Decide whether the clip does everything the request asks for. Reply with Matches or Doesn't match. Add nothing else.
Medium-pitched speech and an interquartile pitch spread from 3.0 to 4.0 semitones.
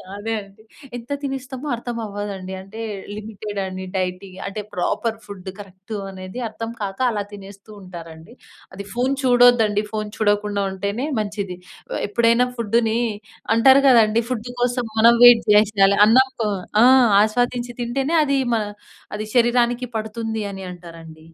Doesn't match